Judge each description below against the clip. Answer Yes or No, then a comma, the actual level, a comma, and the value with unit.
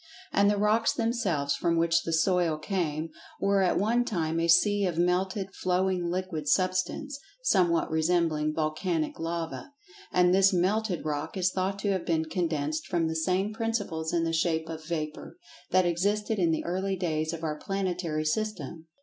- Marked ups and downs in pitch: No, average, 3.3 semitones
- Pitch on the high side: No, medium, 175 Hz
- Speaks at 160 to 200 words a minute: Yes, average, 165 wpm